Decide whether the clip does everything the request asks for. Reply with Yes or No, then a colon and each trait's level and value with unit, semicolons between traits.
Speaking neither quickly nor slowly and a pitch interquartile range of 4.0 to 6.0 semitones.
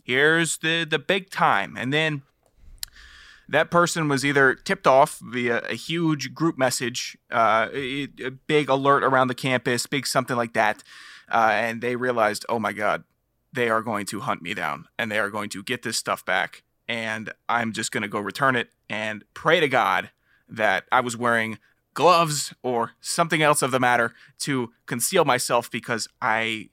No: average, 180 wpm; average, 3.6 semitones